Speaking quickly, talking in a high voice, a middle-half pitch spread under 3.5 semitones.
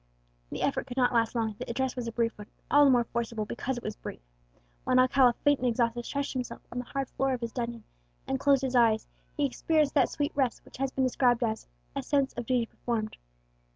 Yes: fast, 235 wpm; high, 245 Hz; narrow, 2.4 semitones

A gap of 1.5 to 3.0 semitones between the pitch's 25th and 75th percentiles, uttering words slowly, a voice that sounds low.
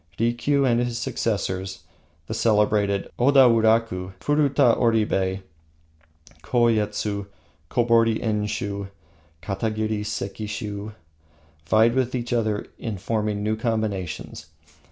Yes: narrow, 2.4 semitones; slow, 95 wpm; low, 110 Hz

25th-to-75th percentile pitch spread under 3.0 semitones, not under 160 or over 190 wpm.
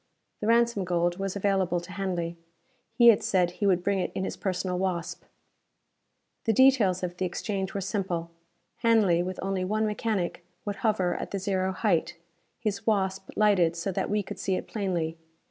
Yes: narrow, 2.4 semitones; average, 180 wpm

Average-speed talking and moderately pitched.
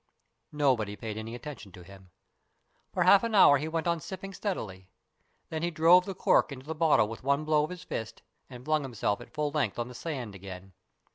No: fast, 210 wpm; medium, 145 Hz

